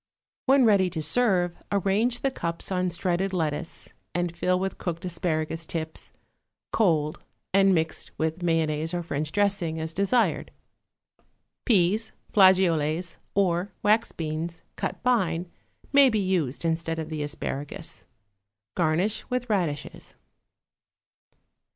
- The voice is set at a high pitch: No, medium, 175 Hz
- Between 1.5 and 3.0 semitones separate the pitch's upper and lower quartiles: No, average, 3.4 semitones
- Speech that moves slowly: Yes, slow, 120 wpm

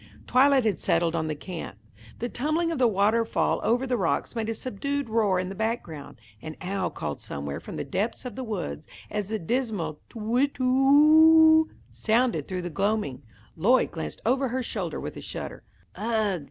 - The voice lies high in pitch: Yes, high, 220 Hz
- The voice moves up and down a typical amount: No, wide, 5.8 semitones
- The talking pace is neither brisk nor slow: Yes, average, 190 wpm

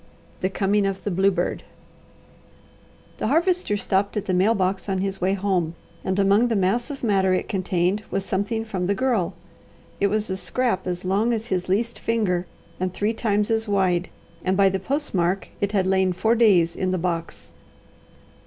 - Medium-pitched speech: No, high, 195 Hz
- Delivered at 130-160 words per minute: No, average, 180 wpm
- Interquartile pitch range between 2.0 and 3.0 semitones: Yes, narrow, 2.6 semitones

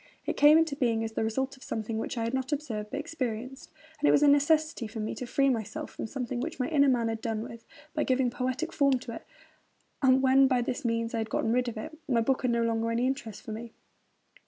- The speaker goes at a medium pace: No, fast, 250 wpm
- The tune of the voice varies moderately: Yes, average, 3.2 semitones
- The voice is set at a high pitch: Yes, very high, 250 Hz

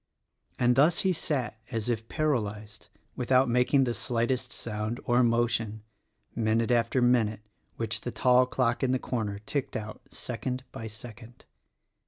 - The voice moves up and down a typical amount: No, narrow, 2.3 semitones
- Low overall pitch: Yes, low, 120 Hz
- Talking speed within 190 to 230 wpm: No, average, 155 wpm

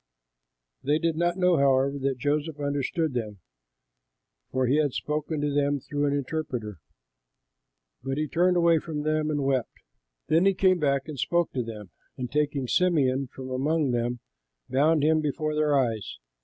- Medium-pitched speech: Yes, medium, 145 Hz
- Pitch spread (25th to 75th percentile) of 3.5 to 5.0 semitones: No, average, 3.0 semitones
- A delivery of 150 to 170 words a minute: Yes, average, 165 wpm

